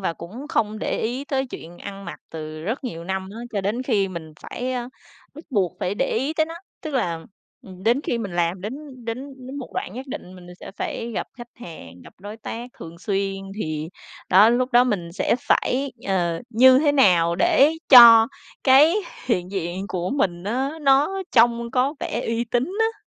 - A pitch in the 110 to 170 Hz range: No, high, 225 Hz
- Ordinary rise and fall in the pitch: No, wide, 5.9 semitones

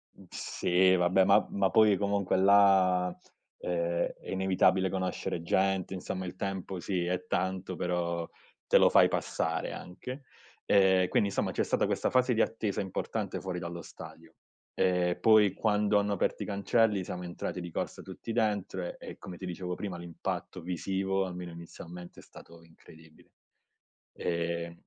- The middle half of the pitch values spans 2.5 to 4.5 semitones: No, narrow, 2.0 semitones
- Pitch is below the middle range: Yes, very low, 95 Hz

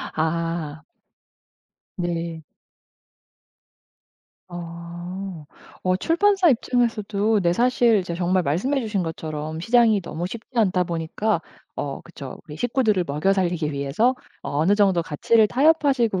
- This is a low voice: No, medium, 185 Hz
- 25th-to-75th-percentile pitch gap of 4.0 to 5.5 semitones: Yes, average, 5.2 semitones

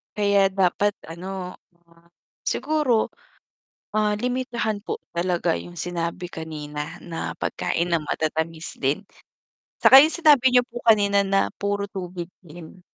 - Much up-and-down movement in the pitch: No, average, 4.0 semitones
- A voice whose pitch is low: No, high, 190 Hz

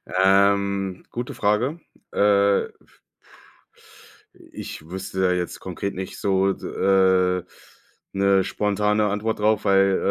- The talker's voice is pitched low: Yes, low, 100 Hz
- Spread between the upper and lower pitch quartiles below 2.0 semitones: Yes, narrow, 1.5 semitones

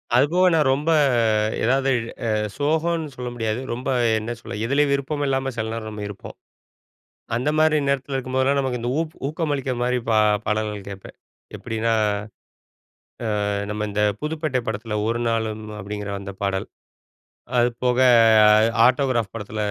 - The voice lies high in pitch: No, low, 125 Hz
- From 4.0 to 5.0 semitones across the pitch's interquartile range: Yes, average, 4.3 semitones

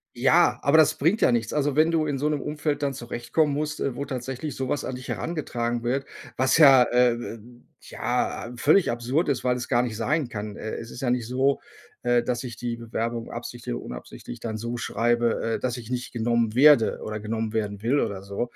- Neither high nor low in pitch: No, low, 120 Hz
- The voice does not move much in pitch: No, average, 3.1 semitones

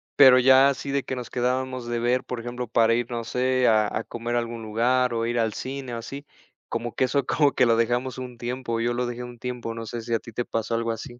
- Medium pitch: No, low, 120 Hz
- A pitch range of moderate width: No, narrow, 1.7 semitones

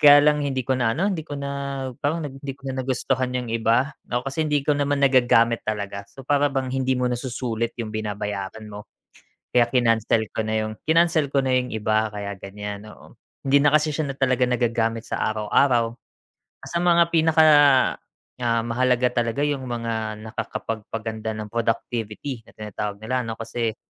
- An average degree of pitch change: Yes, average, 3.9 semitones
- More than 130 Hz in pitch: No, low, 120 Hz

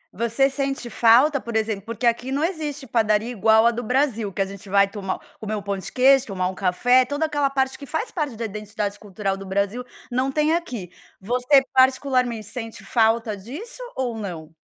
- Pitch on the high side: Yes, high, 235 Hz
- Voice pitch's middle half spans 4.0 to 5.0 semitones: Yes, average, 4.6 semitones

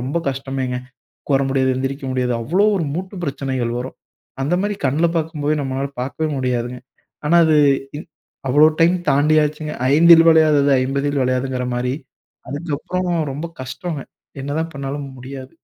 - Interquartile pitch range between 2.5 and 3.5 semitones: Yes, average, 3.2 semitones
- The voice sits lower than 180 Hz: Yes, medium, 140 Hz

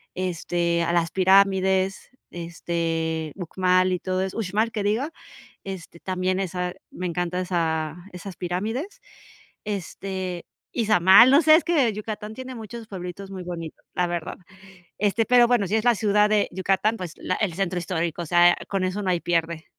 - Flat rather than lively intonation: No, average, 3.2 semitones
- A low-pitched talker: No, medium, 185 Hz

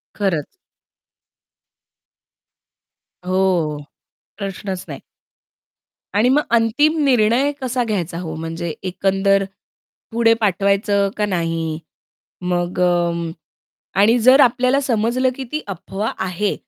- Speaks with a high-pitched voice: Yes, high, 200 Hz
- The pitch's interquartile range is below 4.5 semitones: No, average, 5.1 semitones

